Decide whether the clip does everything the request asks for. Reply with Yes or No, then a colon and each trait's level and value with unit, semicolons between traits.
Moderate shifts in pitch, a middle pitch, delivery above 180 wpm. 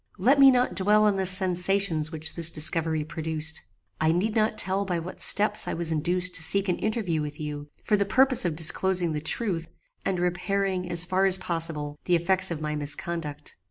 Yes: average, 3.3 semitones; medium, 175 Hz; average, 195 wpm